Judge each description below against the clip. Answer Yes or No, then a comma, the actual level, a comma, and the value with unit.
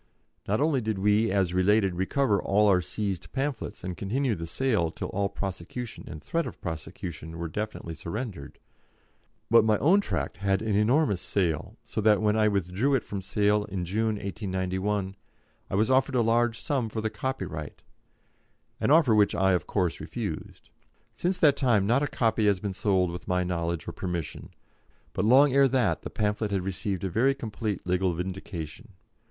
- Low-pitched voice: Yes, low, 105 Hz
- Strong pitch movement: No, average, 3.8 semitones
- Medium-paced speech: Yes, average, 180 wpm